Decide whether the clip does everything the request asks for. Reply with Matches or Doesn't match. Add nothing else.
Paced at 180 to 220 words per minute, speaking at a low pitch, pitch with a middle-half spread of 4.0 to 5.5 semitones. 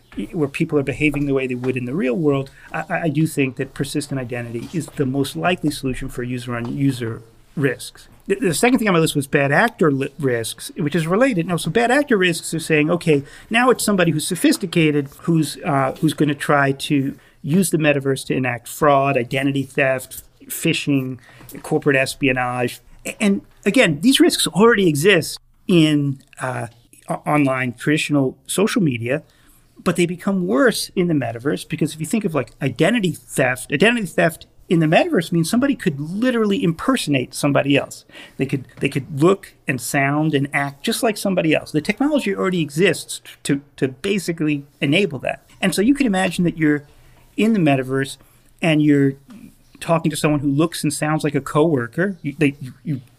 Doesn't match